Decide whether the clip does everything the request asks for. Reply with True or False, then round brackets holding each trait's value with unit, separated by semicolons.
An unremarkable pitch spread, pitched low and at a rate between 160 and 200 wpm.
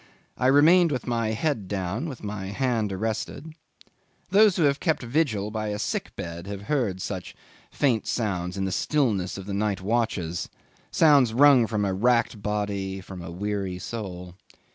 True (4.9 semitones; 105 Hz; 165 wpm)